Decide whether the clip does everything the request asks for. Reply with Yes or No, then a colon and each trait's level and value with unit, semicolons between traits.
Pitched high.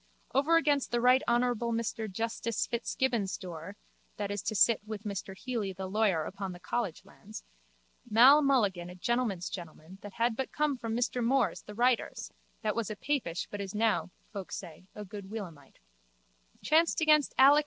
Yes: high, 220 Hz